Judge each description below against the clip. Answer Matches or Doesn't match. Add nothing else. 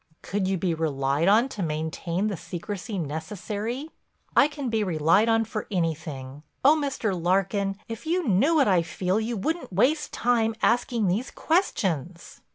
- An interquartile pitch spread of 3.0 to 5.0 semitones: Doesn't match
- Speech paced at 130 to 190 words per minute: Matches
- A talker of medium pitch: Doesn't match